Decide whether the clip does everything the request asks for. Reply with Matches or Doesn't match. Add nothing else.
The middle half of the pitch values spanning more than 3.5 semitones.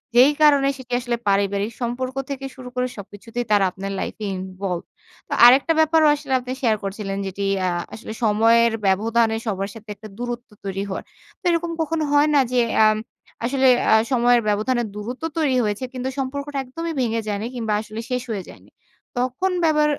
Matches